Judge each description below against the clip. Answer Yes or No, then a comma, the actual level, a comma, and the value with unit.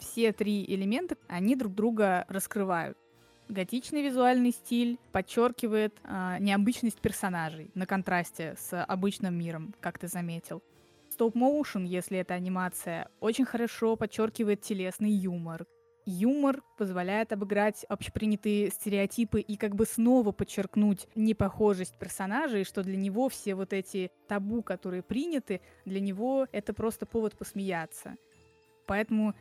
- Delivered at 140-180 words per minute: No, average, 120 wpm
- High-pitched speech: Yes, high, 205 Hz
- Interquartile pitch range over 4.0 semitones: No, average, 3.3 semitones